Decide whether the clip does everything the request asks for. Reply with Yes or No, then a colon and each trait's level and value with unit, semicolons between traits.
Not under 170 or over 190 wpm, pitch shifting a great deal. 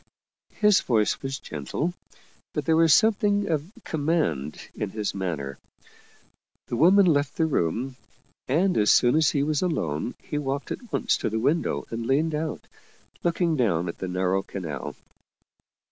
No: average, 160 wpm; wide, 8.6 semitones